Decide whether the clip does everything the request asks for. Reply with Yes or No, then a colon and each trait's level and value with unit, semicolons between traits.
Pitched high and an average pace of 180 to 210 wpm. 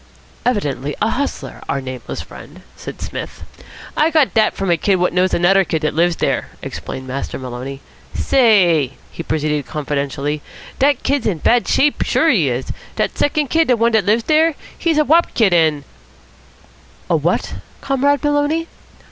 No: high, 195 Hz; average, 165 wpm